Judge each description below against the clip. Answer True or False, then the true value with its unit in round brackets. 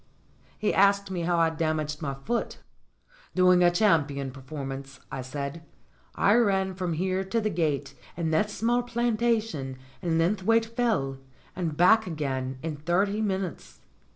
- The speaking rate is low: False (150 wpm)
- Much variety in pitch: True (5.9 semitones)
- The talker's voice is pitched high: False (175 Hz)